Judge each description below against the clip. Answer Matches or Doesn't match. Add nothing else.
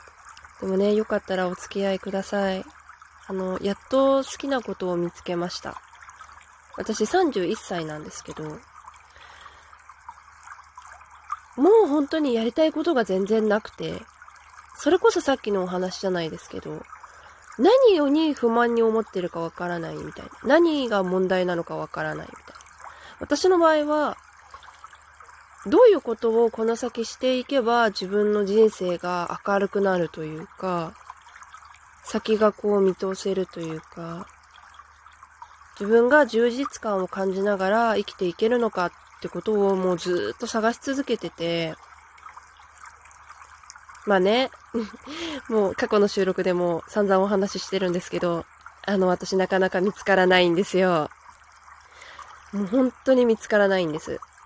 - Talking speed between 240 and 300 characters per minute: Matches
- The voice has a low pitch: Doesn't match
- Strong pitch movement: Doesn't match